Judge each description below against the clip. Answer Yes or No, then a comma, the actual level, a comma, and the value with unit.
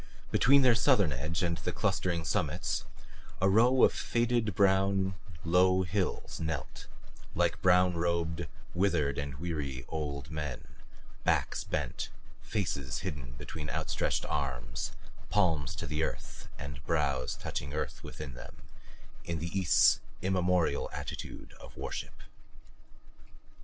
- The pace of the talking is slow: Yes, slow, 120 wpm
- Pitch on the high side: No, very low, 85 Hz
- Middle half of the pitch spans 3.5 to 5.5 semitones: Yes, average, 4.7 semitones